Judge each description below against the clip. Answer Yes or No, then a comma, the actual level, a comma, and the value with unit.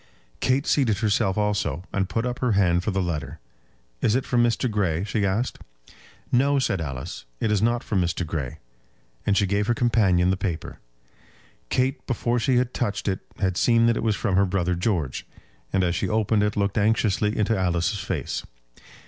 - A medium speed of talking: Yes, average, 190 wpm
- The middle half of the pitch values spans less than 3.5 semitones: No, average, 4.0 semitones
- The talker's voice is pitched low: Yes, low, 105 Hz